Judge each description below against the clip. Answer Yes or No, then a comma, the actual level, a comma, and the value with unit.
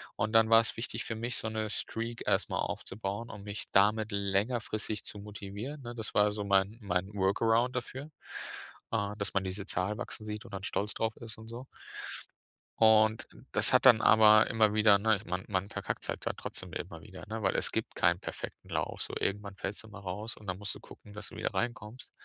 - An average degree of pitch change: No, narrow, 2.1 semitones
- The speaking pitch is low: Yes, low, 105 Hz